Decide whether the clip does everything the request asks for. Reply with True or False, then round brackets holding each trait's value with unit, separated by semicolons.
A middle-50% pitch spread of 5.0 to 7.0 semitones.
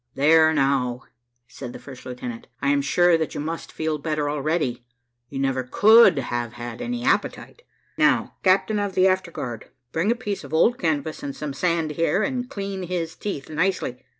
True (5.4 semitones)